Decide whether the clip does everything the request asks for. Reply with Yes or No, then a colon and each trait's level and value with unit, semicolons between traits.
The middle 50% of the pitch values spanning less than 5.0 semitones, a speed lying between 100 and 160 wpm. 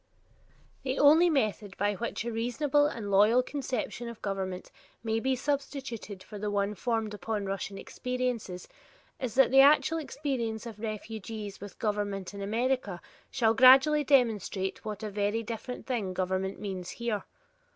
Yes: average, 4.0 semitones; average, 150 wpm